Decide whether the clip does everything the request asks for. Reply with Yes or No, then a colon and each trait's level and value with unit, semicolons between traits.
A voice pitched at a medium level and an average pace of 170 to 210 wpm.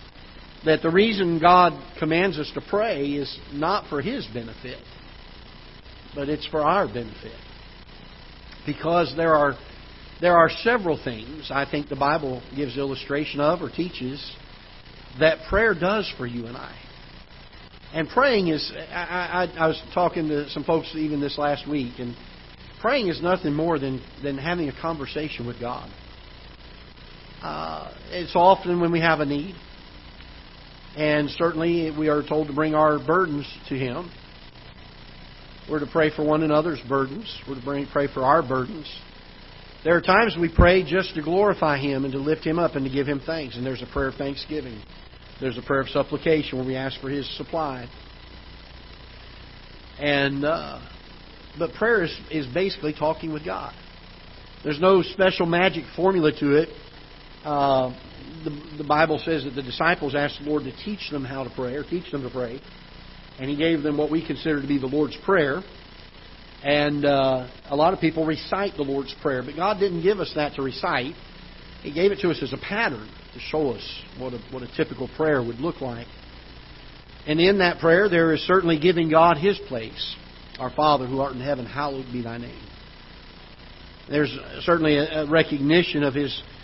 Yes: medium, 145 Hz; average, 175 wpm